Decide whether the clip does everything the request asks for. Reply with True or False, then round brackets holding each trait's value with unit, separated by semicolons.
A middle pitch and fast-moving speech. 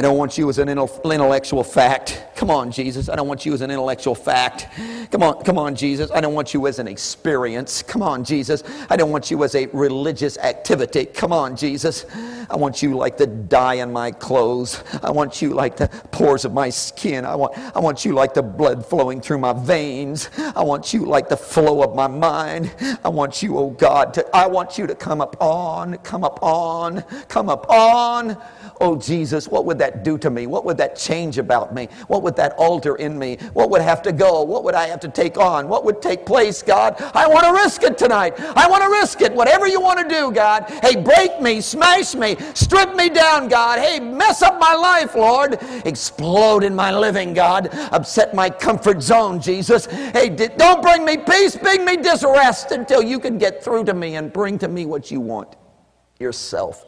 True (180 Hz; 215 wpm)